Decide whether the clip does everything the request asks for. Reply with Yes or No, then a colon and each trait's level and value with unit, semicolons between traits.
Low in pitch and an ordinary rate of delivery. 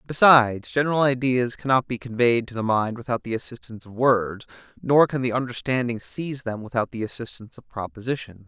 Yes: low, 120 Hz; average, 175 wpm